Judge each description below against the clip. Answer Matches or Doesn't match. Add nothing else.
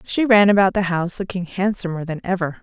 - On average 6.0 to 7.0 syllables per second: Matches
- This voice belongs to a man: Doesn't match